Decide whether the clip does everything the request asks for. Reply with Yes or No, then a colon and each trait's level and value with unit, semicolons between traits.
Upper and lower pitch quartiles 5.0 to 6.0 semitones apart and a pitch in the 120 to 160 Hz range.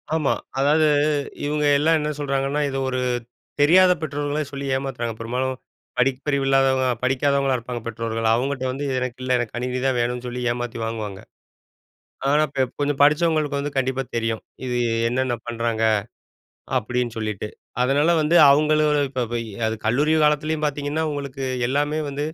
No: average, 3.1 semitones; low, 135 Hz